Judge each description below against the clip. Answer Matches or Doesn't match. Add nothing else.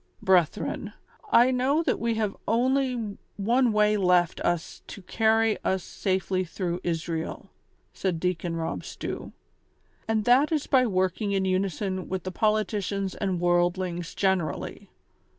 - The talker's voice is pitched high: Matches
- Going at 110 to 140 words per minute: Matches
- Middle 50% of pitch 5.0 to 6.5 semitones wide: Doesn't match